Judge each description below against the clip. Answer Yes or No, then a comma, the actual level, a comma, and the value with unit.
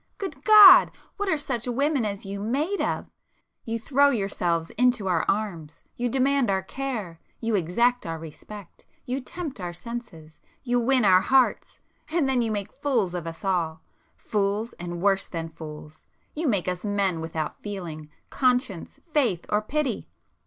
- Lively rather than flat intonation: Yes, wide, 6.7 semitones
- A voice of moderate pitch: No, high, 210 Hz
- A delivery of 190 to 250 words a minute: No, average, 140 wpm